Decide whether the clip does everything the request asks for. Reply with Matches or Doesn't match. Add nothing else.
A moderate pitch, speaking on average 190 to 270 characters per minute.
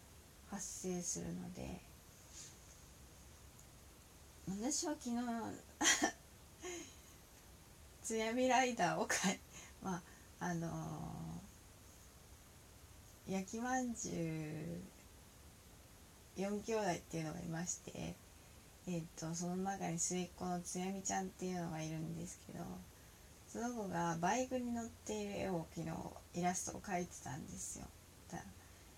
Matches